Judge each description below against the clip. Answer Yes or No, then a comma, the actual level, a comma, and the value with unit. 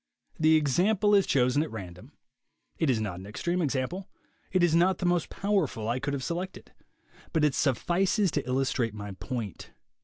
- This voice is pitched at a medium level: Yes, medium, 150 Hz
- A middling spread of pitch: No, wide, 6.4 semitones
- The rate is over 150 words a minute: Yes, average, 175 wpm